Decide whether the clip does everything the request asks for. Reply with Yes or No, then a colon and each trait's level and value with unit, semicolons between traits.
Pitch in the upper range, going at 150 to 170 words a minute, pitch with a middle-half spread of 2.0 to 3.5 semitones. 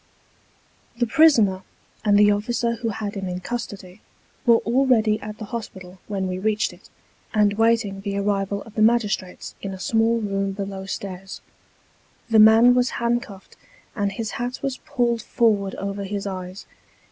Yes: high, 210 Hz; average, 160 wpm; average, 2.8 semitones